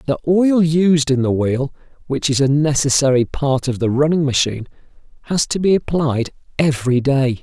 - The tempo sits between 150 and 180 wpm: Yes, average, 170 wpm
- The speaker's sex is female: No, male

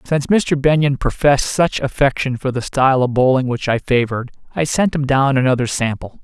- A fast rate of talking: No, average, 195 wpm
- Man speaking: Yes, male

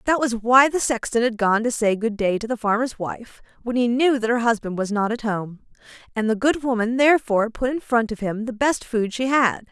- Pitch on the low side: No, high, 235 Hz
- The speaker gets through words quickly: Yes, fast, 245 wpm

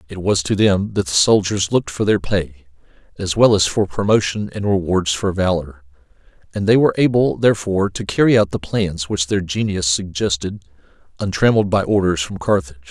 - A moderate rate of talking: Yes, average, 180 wpm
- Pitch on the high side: No, very low, 95 Hz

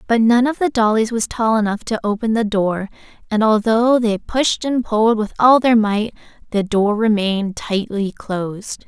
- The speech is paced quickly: No, average, 185 wpm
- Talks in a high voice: Yes, high, 220 Hz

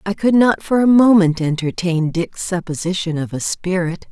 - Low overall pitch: No, medium, 185 Hz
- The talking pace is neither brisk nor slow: Yes, average, 175 wpm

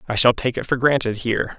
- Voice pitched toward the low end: Yes, low, 120 Hz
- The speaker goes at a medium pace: No, fast, 265 wpm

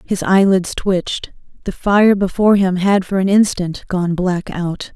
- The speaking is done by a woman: Yes, female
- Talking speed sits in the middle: Yes, average, 170 wpm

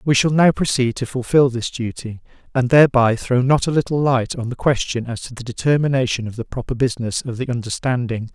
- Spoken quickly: Yes, fast, 210 wpm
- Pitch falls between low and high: No, low, 125 Hz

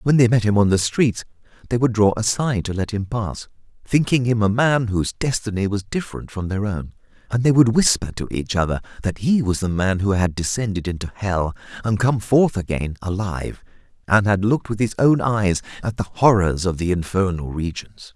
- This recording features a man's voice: Yes, male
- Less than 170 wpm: No, fast, 205 wpm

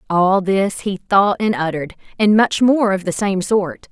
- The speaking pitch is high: Yes, high, 195 Hz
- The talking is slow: No, average, 200 wpm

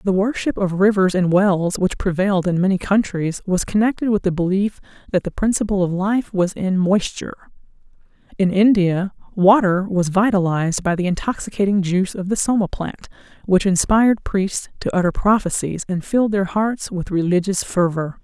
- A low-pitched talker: No, high, 190 Hz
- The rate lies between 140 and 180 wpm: Yes, average, 165 wpm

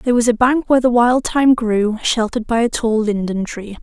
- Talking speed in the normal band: No, fast, 235 wpm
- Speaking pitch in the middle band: No, high, 230 Hz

